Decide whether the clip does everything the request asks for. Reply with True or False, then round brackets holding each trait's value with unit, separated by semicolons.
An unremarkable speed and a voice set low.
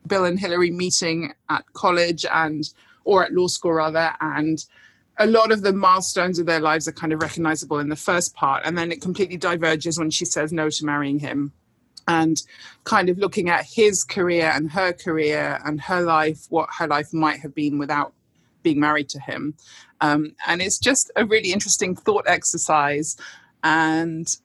False (185 wpm; 165 Hz)